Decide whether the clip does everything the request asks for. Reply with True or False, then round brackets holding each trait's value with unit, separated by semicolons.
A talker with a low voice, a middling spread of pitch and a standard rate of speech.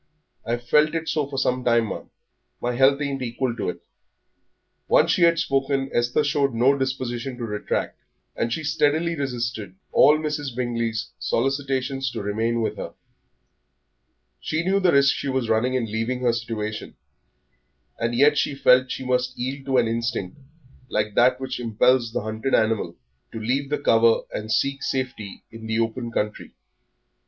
True (125 Hz; 3.1 semitones; 165 wpm)